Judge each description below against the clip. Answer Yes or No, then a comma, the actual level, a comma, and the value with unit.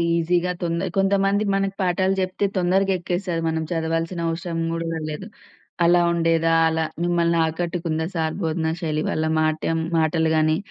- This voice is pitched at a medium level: Yes, medium, 170 Hz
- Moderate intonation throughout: No, narrow, 1.9 semitones